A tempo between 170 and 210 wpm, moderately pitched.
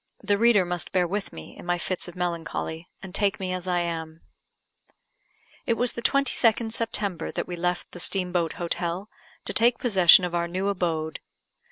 Yes: average, 185 wpm; medium, 180 Hz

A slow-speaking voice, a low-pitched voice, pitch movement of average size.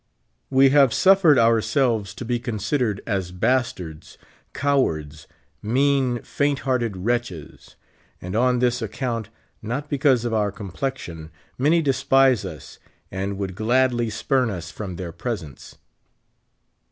Yes: slow, 125 wpm; low, 120 Hz; average, 5.0 semitones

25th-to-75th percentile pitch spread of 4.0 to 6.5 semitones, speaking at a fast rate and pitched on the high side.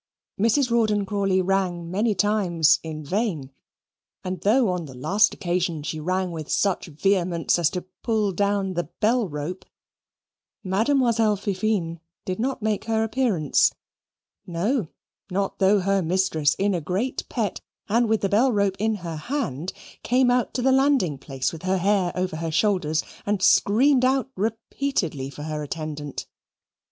No: average, 4.7 semitones; average, 155 wpm; high, 195 Hz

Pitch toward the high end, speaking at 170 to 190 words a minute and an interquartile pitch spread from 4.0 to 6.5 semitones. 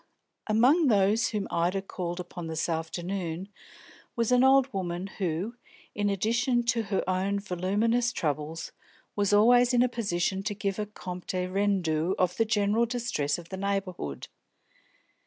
No: high, 195 Hz; average, 145 wpm; average, 4.3 semitones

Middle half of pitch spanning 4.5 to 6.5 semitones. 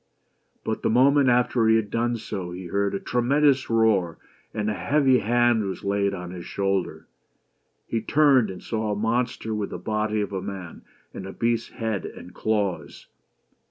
No: average, 3.5 semitones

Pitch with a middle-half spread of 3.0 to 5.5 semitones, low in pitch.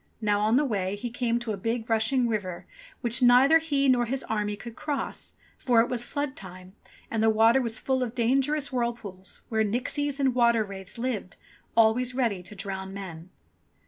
No: average, 3.5 semitones; high, 230 Hz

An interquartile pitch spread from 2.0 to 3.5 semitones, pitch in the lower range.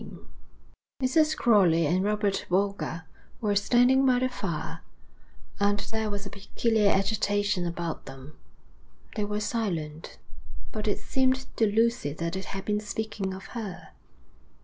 No: average, 3.1 semitones; high, 205 Hz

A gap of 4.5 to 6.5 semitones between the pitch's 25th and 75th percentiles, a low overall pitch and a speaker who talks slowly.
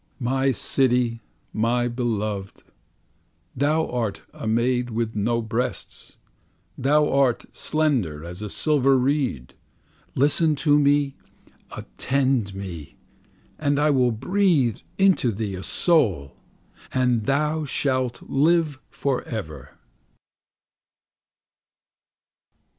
Yes: average, 5.1 semitones; low, 125 Hz; slow, 85 wpm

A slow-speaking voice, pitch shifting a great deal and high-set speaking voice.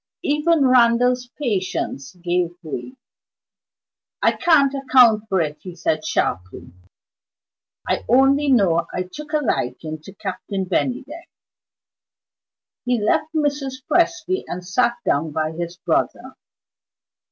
Yes: slow, 115 wpm; wide, 7.9 semitones; high, 235 Hz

